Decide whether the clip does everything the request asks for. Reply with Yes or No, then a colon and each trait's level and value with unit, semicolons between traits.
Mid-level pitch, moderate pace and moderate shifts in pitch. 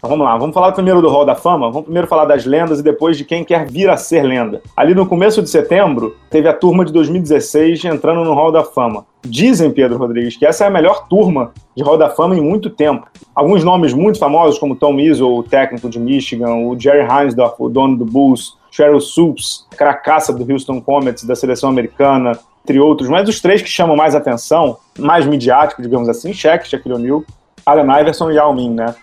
No: medium, 150 Hz; fast, 215 wpm; average, 4.1 semitones